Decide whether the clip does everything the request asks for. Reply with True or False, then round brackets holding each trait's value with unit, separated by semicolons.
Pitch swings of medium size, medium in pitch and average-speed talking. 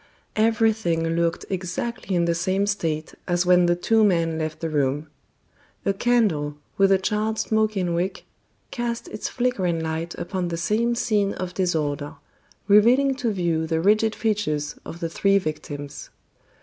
True (4.5 semitones; 180 Hz; 150 wpm)